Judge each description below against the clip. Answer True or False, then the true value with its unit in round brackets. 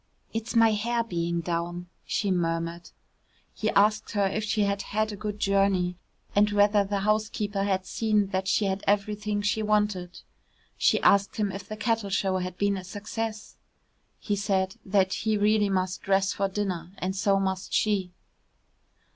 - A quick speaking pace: False (165 wpm)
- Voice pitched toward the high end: True (200 Hz)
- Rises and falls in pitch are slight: True (1.9 semitones)